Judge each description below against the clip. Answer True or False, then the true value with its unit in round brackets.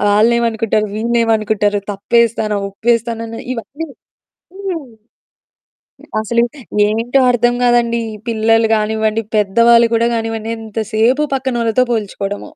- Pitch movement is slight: True (1.5 semitones)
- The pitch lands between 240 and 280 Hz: False (225 Hz)